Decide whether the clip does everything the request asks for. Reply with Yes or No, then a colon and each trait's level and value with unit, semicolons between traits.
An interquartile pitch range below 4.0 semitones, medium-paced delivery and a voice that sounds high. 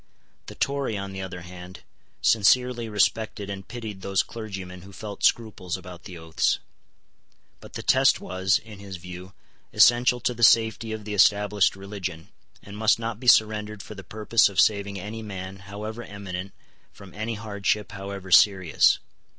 No: narrow, 2.5 semitones; average, 160 wpm; low, 100 Hz